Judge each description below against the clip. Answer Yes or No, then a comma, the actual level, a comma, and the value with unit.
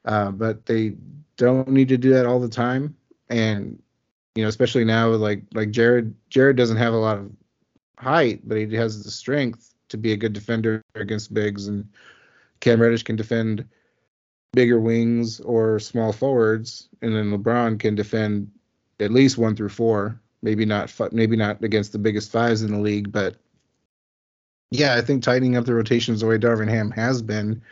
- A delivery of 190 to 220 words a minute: No, average, 180 wpm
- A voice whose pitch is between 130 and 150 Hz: No, low, 115 Hz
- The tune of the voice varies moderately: No, narrow, 1.8 semitones